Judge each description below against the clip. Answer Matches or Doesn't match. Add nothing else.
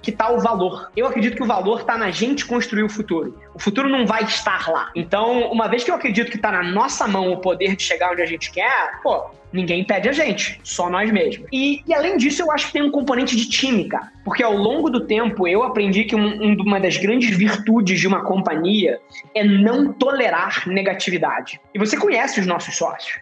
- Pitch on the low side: Doesn't match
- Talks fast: Matches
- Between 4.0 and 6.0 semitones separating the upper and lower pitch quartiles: Matches